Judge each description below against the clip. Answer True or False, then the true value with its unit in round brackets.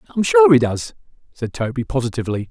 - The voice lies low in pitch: True (120 Hz)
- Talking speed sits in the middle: True (165 wpm)